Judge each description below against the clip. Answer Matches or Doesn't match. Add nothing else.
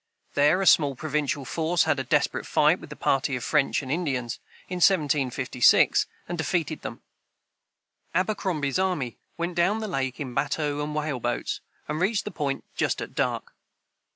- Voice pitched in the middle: Matches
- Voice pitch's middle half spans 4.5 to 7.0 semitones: Doesn't match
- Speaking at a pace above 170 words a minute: Doesn't match